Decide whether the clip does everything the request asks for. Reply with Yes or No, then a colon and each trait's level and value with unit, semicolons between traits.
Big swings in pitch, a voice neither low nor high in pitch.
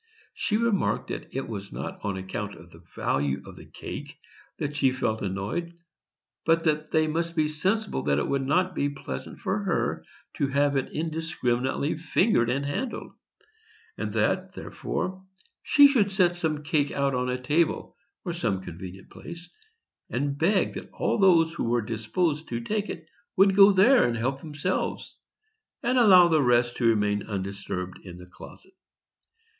Yes: wide, 7.1 semitones; medium, 145 Hz